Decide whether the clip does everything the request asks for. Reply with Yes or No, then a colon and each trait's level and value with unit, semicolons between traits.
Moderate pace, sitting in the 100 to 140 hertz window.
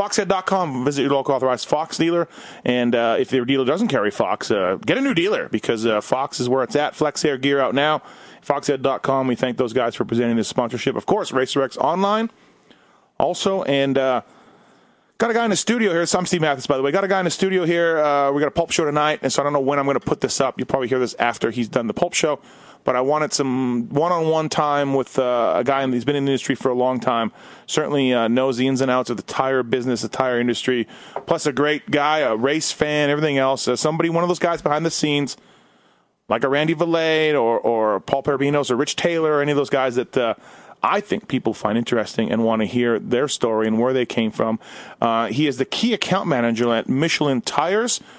No: fast, 245 wpm; low, 135 Hz